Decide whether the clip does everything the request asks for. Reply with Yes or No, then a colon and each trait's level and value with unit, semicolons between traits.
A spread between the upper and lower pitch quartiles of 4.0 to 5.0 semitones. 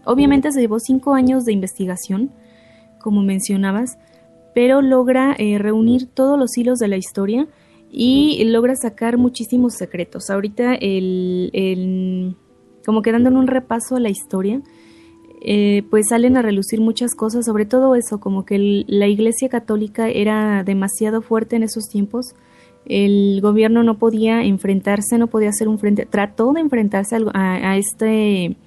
No: average, 3.3 semitones